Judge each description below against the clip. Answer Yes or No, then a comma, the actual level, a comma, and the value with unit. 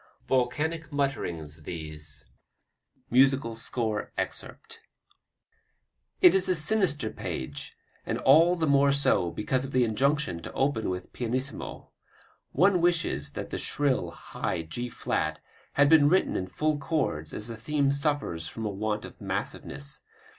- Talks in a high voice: No, low, 135 Hz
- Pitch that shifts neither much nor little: No, wide, 6.2 semitones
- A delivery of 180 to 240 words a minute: No, average, 140 wpm